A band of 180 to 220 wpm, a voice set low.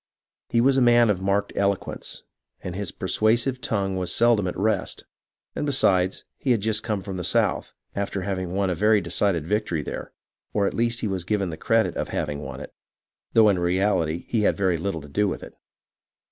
Yes: fast, 205 wpm; low, 100 Hz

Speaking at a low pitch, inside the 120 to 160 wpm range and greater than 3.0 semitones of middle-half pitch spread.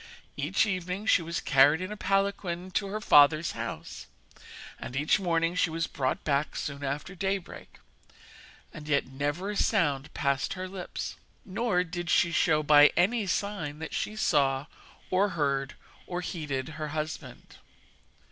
No: medium, 165 Hz; average, 150 wpm; average, 4.3 semitones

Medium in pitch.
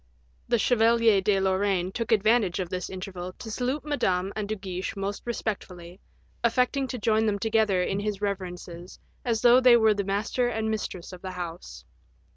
No: high, 205 Hz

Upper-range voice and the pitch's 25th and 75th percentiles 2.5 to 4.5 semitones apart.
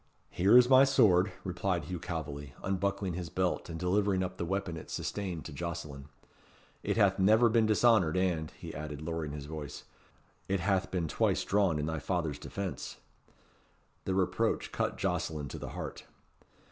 No: very low, 90 Hz; average, 3.6 semitones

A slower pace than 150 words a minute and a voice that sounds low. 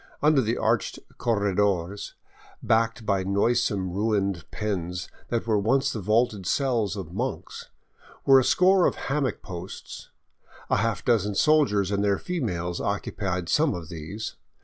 Yes: average, 140 wpm; low, 105 Hz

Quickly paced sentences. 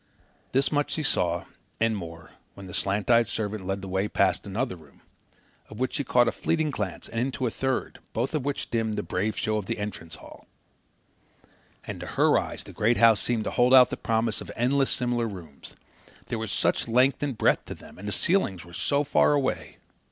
Yes: fast, 210 wpm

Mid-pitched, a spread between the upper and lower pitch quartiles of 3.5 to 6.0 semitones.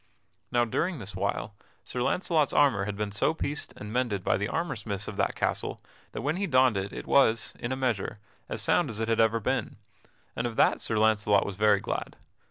No: low, 110 Hz; average, 4.2 semitones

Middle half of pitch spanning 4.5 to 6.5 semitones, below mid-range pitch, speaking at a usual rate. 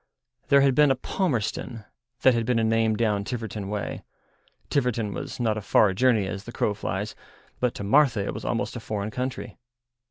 No: average, 3.4 semitones; low, 115 Hz; average, 190 wpm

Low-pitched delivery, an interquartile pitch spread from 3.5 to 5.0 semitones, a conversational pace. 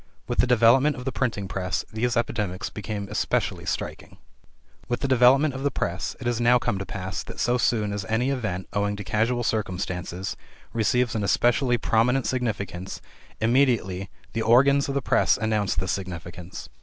Yes: low, 115 Hz; average, 4.1 semitones; average, 170 wpm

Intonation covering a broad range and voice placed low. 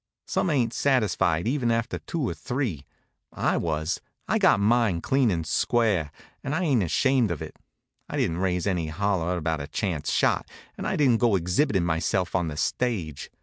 Yes: wide, 6.6 semitones; low, 100 Hz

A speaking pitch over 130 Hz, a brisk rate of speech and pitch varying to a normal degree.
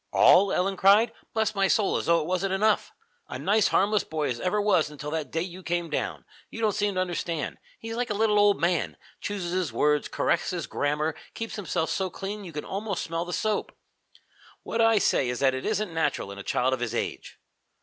Yes: medium, 185 Hz; fast, 220 wpm; average, 4.5 semitones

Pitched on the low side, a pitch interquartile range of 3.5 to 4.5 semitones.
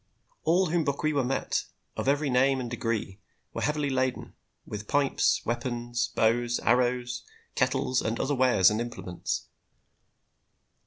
No: low, 125 Hz; average, 2.7 semitones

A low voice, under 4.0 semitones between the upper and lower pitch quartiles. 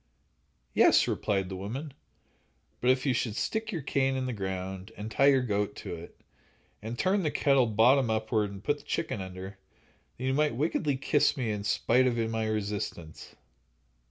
No: low, 115 Hz; average, 5.0 semitones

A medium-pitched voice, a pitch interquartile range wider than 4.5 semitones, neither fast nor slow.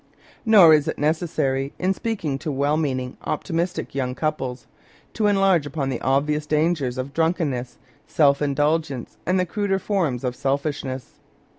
No: medium, 150 Hz; average, 3.8 semitones; average, 145 wpm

